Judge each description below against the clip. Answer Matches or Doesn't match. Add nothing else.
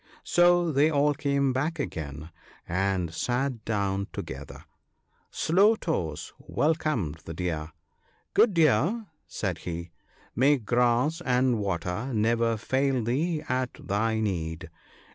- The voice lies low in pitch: Matches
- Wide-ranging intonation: Matches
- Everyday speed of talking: Doesn't match